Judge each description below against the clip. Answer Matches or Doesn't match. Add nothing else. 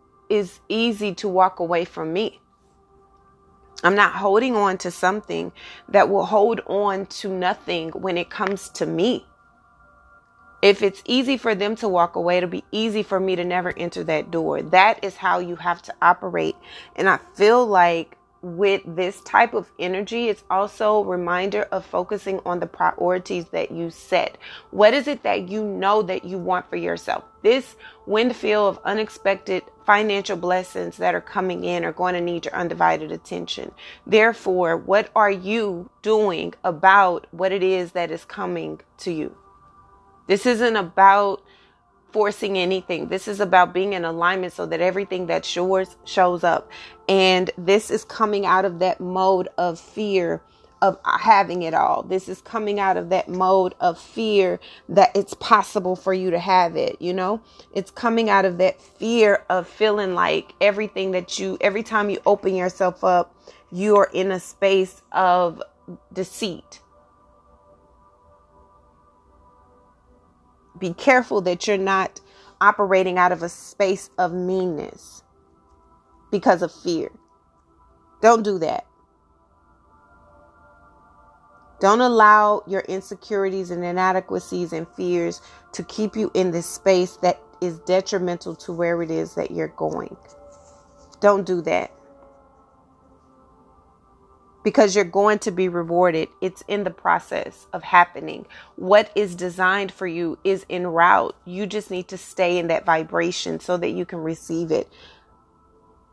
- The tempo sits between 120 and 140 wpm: Doesn't match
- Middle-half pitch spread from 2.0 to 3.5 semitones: Matches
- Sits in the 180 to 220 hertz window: Matches